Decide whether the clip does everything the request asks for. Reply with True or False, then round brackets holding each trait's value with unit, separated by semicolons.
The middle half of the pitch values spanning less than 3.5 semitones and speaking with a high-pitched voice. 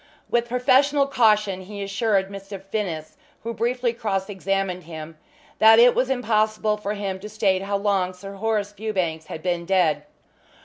True (2.8 semitones; 200 Hz)